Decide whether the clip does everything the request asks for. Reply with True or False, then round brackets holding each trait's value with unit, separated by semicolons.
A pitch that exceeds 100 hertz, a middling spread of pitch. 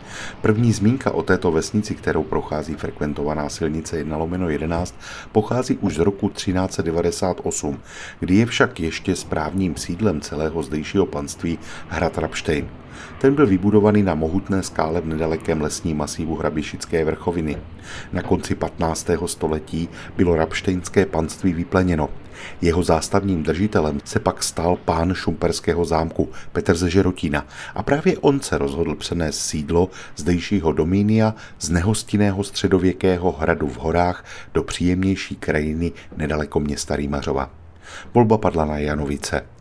False (85 Hz; 3.6 semitones)